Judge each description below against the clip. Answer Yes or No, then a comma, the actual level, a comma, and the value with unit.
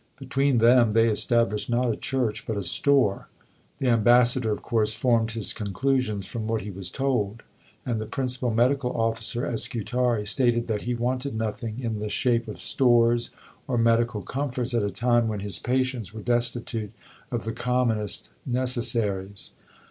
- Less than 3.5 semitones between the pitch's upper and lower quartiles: Yes, narrow, 2.4 semitones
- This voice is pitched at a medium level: No, low, 115 Hz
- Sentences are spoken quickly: No, average, 165 wpm